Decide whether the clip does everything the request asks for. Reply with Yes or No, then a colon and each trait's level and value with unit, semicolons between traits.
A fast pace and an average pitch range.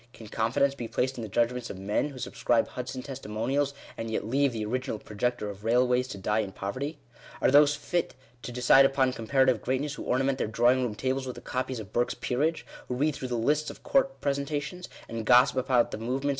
Yes: fast, 215 wpm; average, 3.1 semitones